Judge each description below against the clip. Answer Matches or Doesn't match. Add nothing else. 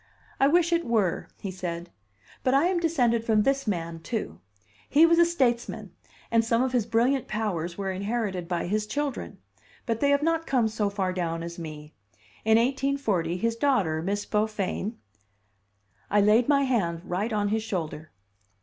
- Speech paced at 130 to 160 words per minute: Doesn't match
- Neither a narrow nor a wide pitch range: Doesn't match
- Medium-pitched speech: Doesn't match